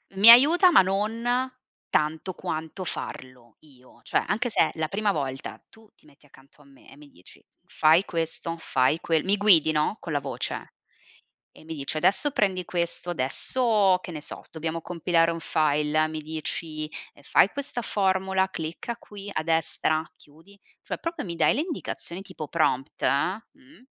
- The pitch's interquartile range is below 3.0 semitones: No, average, 4.9 semitones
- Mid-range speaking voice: Yes, medium, 165 Hz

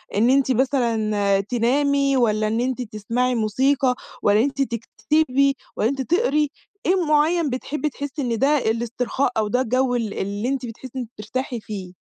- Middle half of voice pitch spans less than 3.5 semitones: No, average, 3.9 semitones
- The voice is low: No, very high, 250 Hz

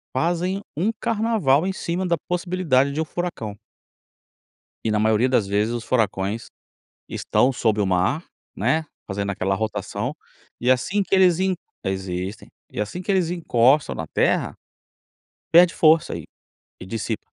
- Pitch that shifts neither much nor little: No, wide, 8.8 semitones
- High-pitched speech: No, low, 130 Hz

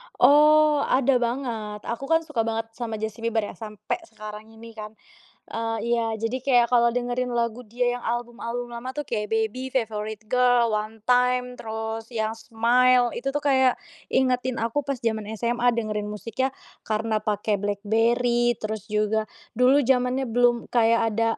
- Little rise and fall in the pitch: Yes, narrow, 2.2 semitones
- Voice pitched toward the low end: No, high, 235 Hz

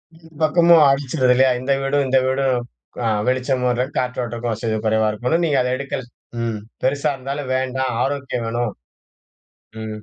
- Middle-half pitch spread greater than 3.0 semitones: No, narrow, 2.4 semitones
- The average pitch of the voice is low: Yes, low, 130 Hz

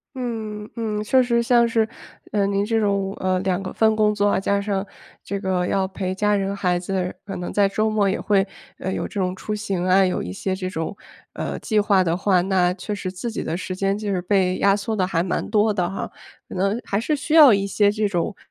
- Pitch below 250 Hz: Yes, high, 200 Hz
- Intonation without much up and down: Yes, narrow, 2.2 semitones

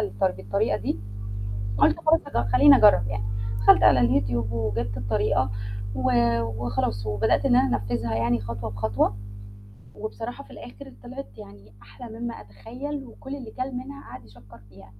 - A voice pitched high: No, low, 115 Hz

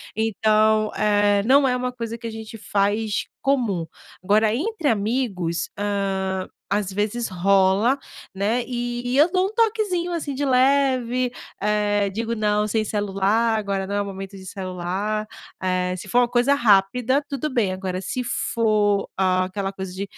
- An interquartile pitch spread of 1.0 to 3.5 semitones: No, average, 3.9 semitones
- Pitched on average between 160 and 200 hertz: No, high, 215 Hz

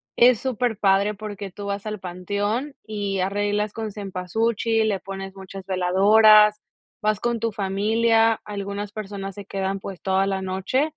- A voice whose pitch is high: Yes, high, 205 Hz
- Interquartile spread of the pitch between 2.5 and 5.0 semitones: No, narrow, 2.0 semitones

